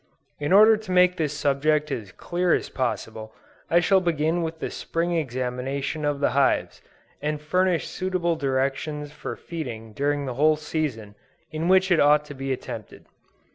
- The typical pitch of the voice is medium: Yes, medium, 150 Hz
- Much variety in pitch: No, average, 4.0 semitones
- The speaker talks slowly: No, average, 165 wpm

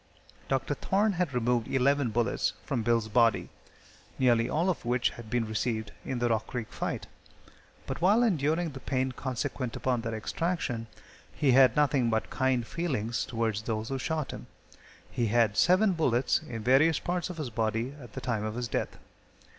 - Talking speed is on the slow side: No, average, 175 wpm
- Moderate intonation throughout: Yes, average, 4.1 semitones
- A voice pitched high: No, low, 125 Hz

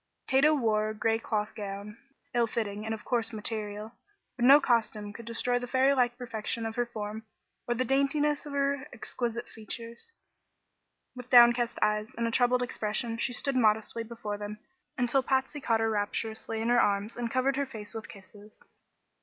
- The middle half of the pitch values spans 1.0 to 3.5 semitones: Yes, narrow, 2.6 semitones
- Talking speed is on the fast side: No, average, 180 wpm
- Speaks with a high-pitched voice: Yes, high, 230 Hz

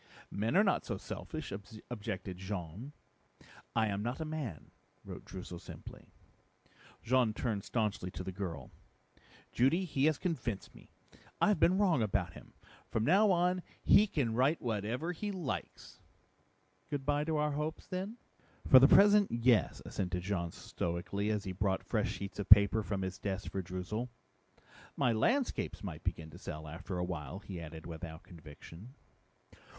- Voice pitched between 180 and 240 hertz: No, low, 110 Hz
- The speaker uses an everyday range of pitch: No, wide, 8.2 semitones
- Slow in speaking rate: No, average, 160 wpm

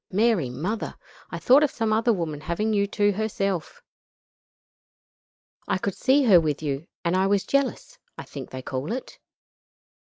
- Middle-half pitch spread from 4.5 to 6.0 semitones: Yes, wide, 5.4 semitones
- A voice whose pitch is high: Yes, high, 200 Hz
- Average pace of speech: Yes, average, 160 wpm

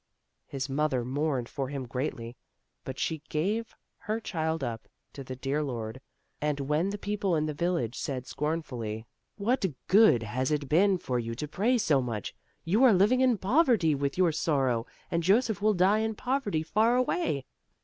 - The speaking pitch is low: No, medium, 155 Hz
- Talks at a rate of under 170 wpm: No, average, 180 wpm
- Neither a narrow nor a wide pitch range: No, wide, 7.6 semitones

